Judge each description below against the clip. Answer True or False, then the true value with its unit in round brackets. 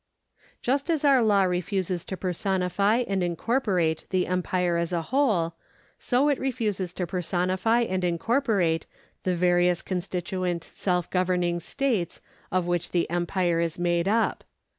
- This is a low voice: False (180 Hz)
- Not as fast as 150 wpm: True (140 wpm)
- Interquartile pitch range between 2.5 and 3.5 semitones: True (3.2 semitones)